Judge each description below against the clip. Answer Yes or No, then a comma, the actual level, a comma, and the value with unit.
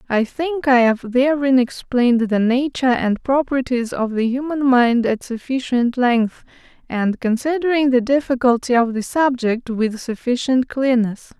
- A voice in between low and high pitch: No, very high, 250 Hz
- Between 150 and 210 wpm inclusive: No, average, 140 wpm